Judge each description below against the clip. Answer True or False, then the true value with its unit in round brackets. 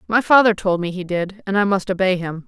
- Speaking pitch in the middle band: False (195 Hz)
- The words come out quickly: True (265 wpm)